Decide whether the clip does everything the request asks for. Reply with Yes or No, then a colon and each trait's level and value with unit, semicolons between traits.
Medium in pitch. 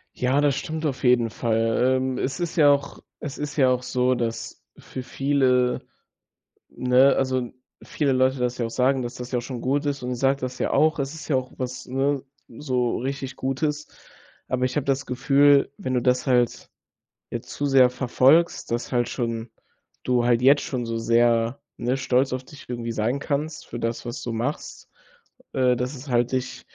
No: low, 130 Hz